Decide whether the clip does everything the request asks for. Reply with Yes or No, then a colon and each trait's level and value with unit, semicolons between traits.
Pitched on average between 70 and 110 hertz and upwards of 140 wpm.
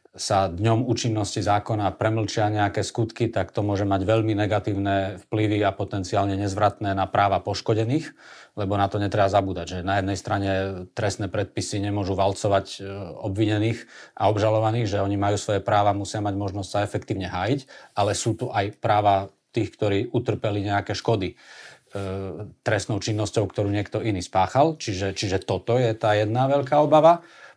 Yes: low, 105 Hz; average, 155 wpm